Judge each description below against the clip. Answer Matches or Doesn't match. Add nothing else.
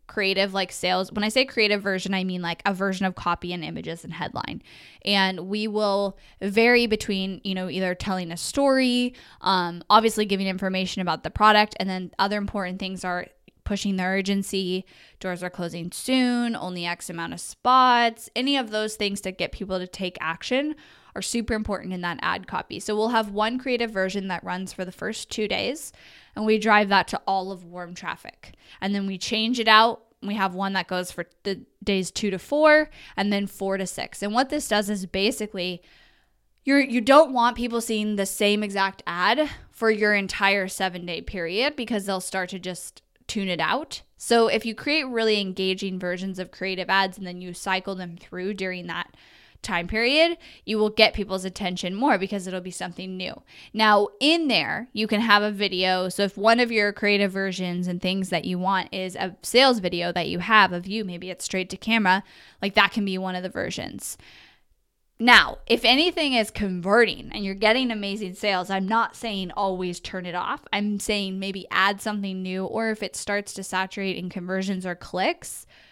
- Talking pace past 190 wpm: Matches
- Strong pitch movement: Doesn't match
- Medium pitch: Doesn't match